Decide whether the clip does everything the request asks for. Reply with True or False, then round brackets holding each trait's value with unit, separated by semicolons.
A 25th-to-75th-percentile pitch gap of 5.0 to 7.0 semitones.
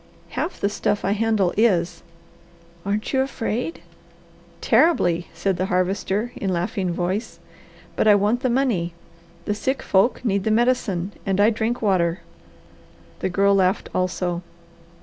False (3.8 semitones)